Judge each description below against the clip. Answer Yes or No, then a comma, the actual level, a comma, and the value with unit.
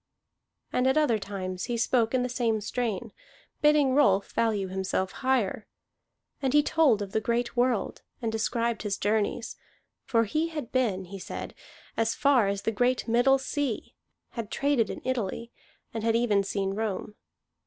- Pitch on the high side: Yes, high, 230 Hz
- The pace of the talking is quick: No, average, 165 wpm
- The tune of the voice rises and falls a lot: No, average, 3.9 semitones